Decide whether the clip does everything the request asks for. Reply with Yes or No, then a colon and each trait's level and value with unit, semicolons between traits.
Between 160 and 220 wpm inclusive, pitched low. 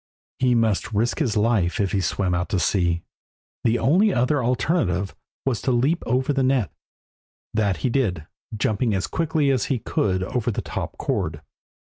Yes: average, 170 wpm; low, 115 Hz